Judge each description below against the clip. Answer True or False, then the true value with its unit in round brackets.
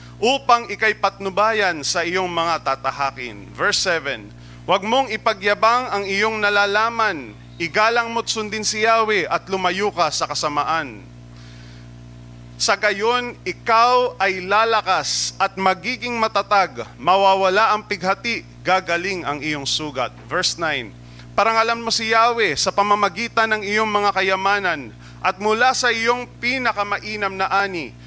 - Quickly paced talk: False (125 wpm)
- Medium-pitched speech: False (200 Hz)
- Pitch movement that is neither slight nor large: False (6.1 semitones)